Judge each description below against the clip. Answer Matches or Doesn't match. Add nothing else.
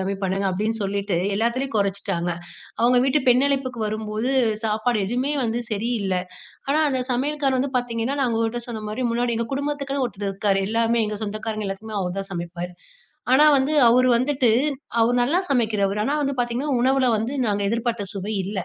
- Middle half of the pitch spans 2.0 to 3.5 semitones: Doesn't match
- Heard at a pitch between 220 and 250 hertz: Matches